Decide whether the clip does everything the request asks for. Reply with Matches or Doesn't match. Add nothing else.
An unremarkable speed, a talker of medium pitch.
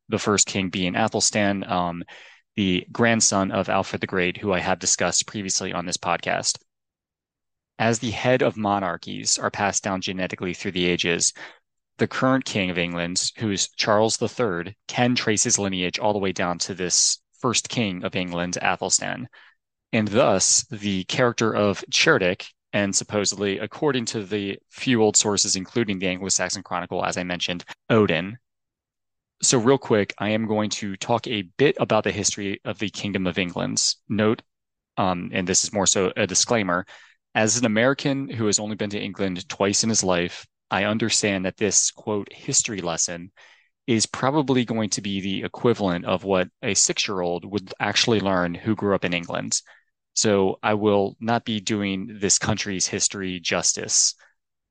Doesn't match